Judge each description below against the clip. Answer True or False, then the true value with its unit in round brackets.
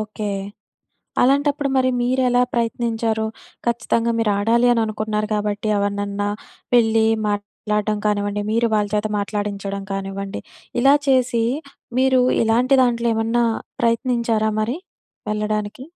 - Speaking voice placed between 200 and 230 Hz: True (220 Hz)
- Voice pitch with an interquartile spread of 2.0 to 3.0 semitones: True (2.4 semitones)